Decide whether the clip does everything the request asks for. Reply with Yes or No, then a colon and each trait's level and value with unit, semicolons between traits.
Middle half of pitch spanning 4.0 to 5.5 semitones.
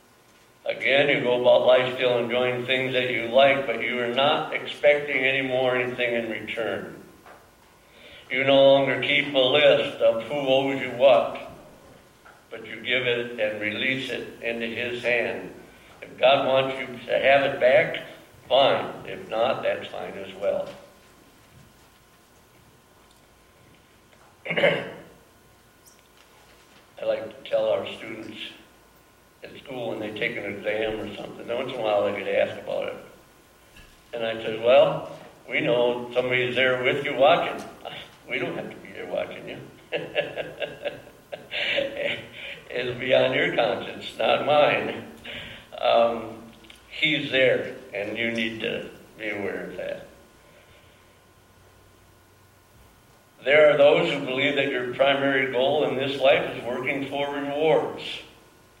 No: average, 2.9 semitones